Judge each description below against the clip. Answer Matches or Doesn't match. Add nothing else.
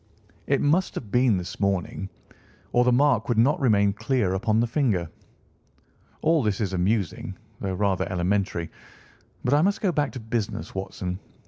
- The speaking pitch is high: Doesn't match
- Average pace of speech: Matches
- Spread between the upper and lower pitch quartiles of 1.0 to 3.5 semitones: Doesn't match